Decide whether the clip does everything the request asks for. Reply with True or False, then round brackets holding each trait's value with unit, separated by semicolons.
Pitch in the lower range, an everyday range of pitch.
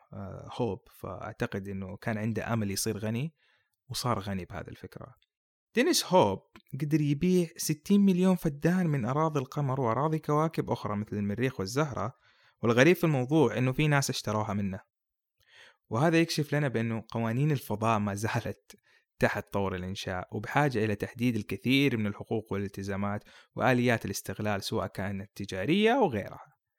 False (115 Hz; 6.3 semitones)